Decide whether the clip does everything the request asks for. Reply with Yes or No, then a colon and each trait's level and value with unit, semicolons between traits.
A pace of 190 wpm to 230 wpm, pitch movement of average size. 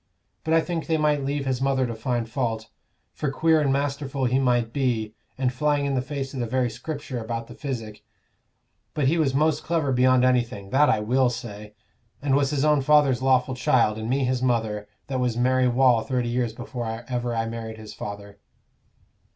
Yes: average, 200 wpm; average, 3.1 semitones